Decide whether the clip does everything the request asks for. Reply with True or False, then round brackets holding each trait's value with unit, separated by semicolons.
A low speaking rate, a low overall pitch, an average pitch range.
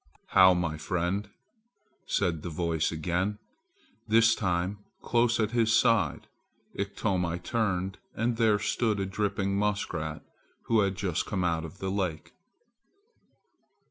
True (125 wpm; 95 Hz; 3.3 semitones)